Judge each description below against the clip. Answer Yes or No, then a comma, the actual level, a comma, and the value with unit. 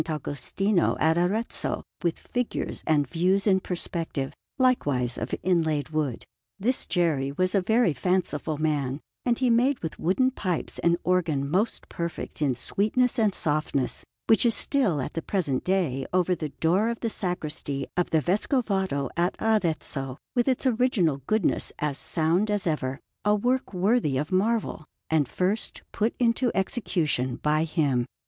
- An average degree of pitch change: No, wide, 6.0 semitones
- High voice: No, medium, 175 Hz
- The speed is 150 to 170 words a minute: Yes, average, 155 wpm